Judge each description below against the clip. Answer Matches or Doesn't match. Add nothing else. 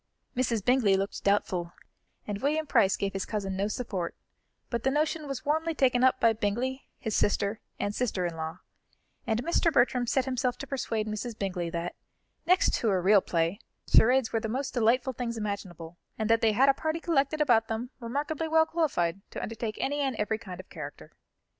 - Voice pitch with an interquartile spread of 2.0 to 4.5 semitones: Doesn't match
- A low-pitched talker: Doesn't match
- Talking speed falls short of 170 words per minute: Doesn't match